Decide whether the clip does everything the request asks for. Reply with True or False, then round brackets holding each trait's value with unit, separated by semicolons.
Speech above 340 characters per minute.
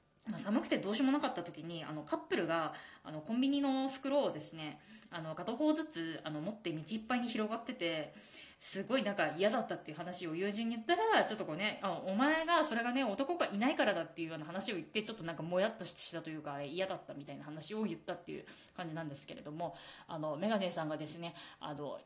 True (465 characters per minute)